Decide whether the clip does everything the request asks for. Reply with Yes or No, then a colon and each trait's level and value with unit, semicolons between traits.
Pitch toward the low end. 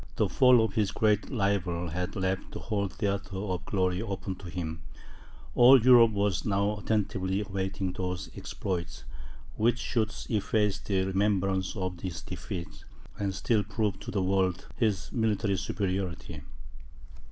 Yes: low, 100 Hz